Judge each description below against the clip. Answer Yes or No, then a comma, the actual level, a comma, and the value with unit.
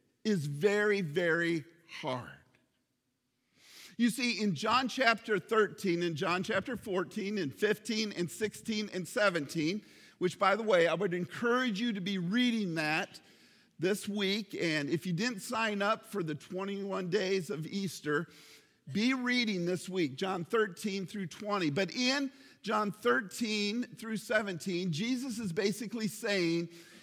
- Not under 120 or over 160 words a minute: Yes, average, 140 wpm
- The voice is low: No, high, 200 Hz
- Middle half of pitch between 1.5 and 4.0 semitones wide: Yes, average, 3.7 semitones